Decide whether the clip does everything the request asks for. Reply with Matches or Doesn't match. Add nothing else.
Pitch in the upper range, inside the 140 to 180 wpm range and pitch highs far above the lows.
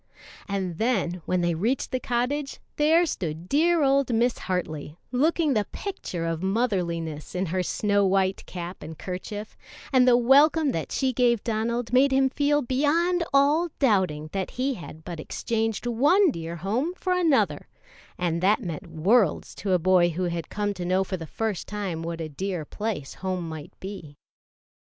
Matches